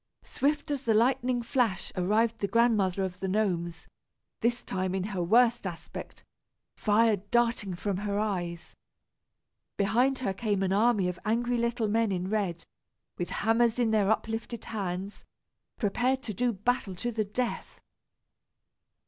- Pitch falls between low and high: No, high, 215 Hz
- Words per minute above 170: No, average, 145 wpm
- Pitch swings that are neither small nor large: Yes, average, 3.7 semitones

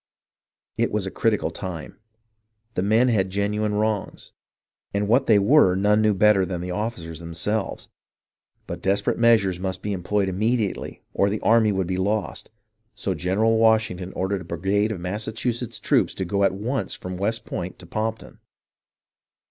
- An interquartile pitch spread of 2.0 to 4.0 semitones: Yes, average, 2.8 semitones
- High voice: No, low, 100 Hz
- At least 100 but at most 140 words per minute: No, average, 160 wpm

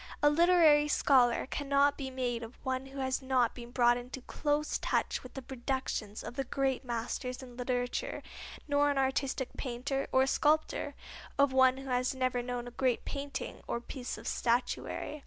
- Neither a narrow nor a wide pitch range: No, narrow, 2.2 semitones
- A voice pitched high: Yes, very high, 260 Hz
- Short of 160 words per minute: No, average, 175 wpm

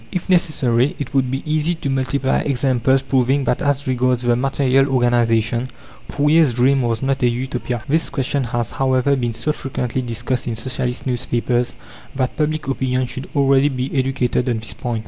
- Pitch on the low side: Yes, low, 130 Hz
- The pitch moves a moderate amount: No, narrow, 2.1 semitones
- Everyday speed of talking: Yes, average, 170 wpm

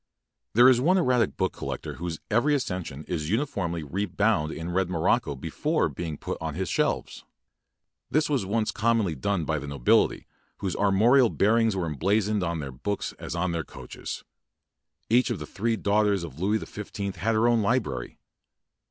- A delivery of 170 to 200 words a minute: Yes, average, 180 wpm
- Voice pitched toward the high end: No, low, 100 Hz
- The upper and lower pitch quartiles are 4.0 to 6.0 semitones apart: Yes, average, 5.2 semitones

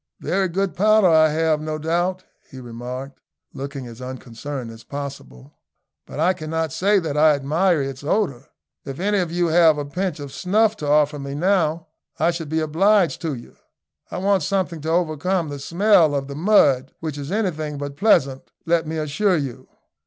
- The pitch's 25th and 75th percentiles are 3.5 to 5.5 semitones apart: Yes, average, 4.3 semitones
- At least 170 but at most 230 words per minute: Yes, average, 180 wpm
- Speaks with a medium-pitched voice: Yes, medium, 155 Hz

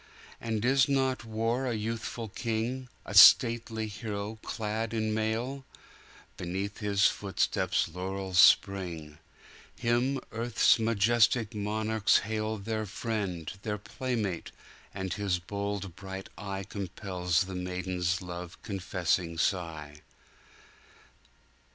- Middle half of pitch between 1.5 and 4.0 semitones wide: Yes, average, 3.4 semitones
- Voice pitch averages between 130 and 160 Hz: No, low, 105 Hz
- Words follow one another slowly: Yes, slow, 90 wpm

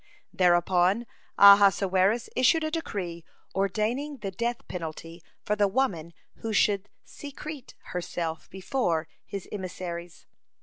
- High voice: Yes, high, 195 Hz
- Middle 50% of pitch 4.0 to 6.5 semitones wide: Yes, average, 4.9 semitones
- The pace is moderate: No, slow, 105 wpm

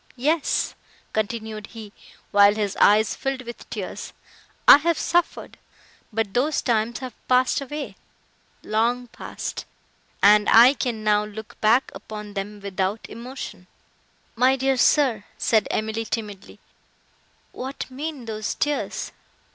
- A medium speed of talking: No, slow, 115 wpm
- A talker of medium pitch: No, high, 225 Hz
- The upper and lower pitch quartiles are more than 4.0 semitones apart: No, average, 3.6 semitones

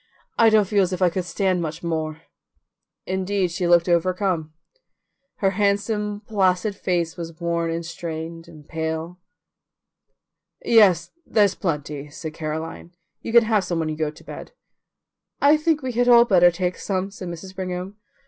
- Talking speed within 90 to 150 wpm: No, average, 160 wpm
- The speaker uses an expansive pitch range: No, average, 3.5 semitones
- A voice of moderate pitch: Yes, medium, 180 Hz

